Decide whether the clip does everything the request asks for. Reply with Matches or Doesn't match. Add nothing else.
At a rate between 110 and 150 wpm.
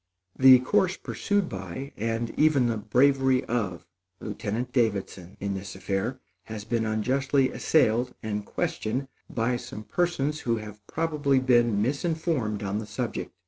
Matches